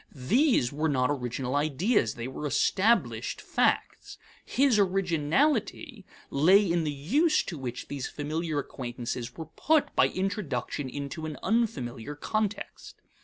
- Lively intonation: Yes, wide, 7.3 semitones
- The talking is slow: Yes, slow, 125 wpm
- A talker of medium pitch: Yes, medium, 155 Hz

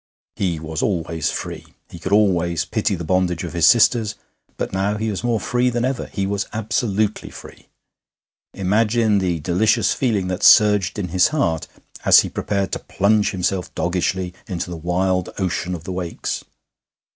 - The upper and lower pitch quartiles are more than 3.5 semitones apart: No, average, 3.2 semitones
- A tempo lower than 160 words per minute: No, average, 170 wpm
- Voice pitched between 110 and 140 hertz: No, very low, 95 Hz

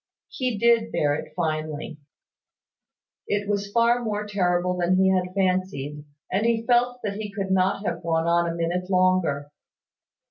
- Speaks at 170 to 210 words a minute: No, average, 155 wpm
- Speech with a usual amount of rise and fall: Yes, average, 3.5 semitones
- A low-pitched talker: No, medium, 185 Hz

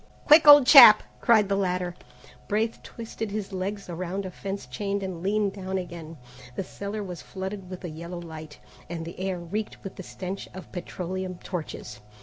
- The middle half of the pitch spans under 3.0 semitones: Yes, narrow, 2.4 semitones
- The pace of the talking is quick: No, average, 175 wpm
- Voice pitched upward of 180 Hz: Yes, high, 190 Hz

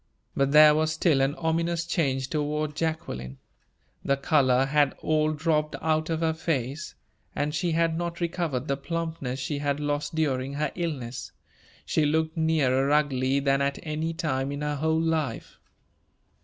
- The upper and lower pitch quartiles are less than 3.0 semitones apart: Yes, narrow, 2.6 semitones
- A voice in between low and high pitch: Yes, medium, 150 Hz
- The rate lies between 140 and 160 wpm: Yes, average, 155 wpm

